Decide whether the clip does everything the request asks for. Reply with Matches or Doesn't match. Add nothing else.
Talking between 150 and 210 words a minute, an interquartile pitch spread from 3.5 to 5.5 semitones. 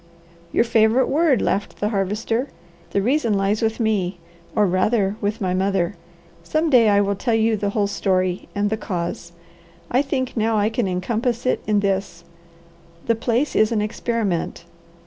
Doesn't match